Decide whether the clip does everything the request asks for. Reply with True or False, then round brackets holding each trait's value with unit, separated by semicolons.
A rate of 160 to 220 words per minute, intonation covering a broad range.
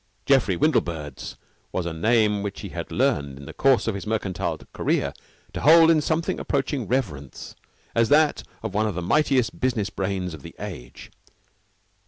True (170 wpm; 7.3 semitones)